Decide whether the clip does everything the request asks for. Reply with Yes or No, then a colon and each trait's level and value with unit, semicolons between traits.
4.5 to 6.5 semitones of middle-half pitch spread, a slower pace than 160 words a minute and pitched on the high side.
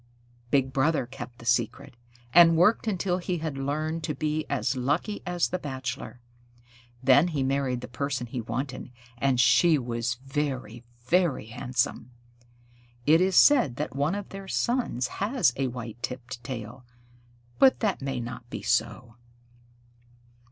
No: average, 5.1 semitones; average, 145 wpm; low, 135 Hz